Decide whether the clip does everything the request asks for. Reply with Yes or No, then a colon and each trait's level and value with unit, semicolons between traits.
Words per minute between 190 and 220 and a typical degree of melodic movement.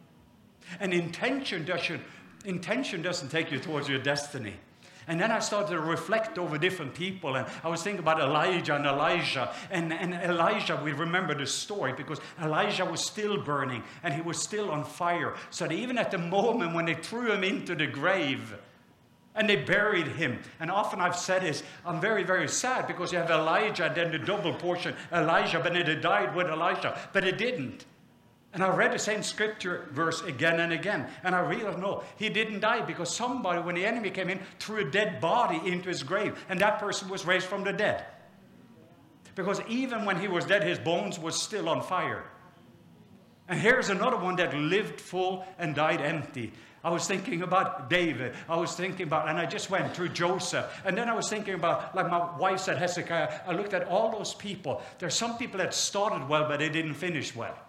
Yes: average, 200 wpm; average, 3.4 semitones